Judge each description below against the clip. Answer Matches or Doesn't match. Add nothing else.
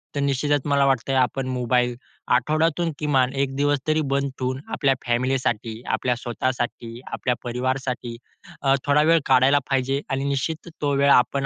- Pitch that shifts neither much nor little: Doesn't match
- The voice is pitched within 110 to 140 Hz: Matches